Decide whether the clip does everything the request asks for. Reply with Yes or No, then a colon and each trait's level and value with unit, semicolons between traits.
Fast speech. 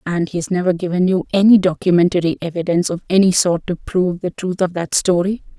No: average, 195 wpm